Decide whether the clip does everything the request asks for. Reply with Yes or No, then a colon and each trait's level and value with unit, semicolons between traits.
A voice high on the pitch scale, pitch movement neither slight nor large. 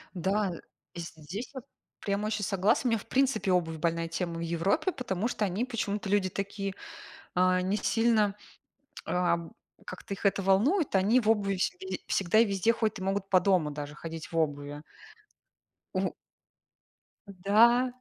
Yes: high, 195 Hz; average, 3.4 semitones